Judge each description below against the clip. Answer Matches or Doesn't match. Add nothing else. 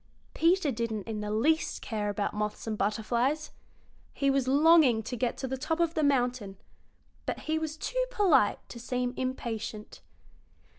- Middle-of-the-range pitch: Doesn't match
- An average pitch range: Doesn't match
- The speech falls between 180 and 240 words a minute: Doesn't match